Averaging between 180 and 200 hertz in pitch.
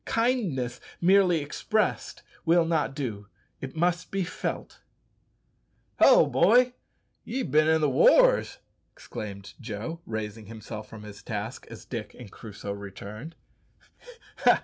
No: low, 135 Hz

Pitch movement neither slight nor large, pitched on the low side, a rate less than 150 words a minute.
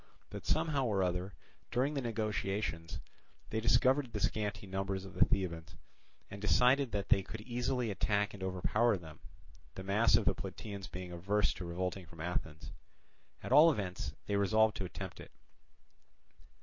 No: average, 3.3 semitones; low, 100 Hz; average, 160 wpm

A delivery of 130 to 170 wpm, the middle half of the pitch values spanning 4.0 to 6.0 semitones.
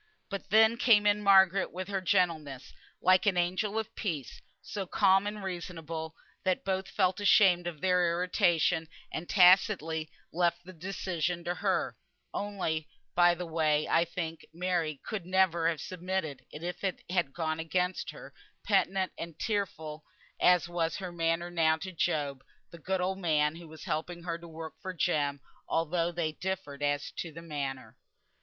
No: average, 165 wpm; average, 2.8 semitones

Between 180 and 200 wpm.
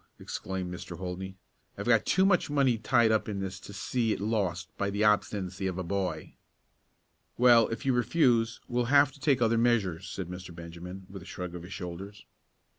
Yes: average, 195 wpm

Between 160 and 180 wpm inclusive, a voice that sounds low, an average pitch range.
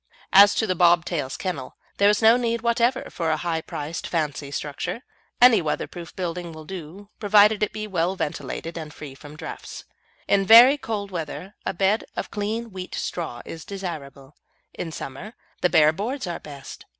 No: average, 175 wpm; medium, 180 Hz; average, 4.9 semitones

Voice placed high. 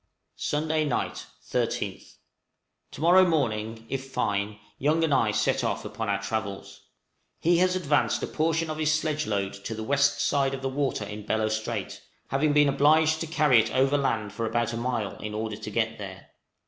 No: low, 130 Hz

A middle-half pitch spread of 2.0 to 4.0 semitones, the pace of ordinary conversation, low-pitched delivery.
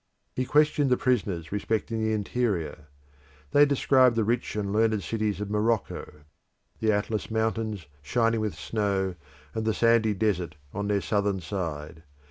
Yes: narrow, 2.4 semitones; average, 145 wpm; low, 110 Hz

